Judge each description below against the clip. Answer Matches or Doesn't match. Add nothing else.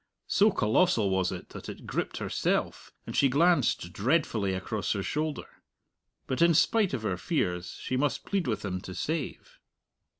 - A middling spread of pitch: Doesn't match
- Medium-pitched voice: Doesn't match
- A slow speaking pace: Doesn't match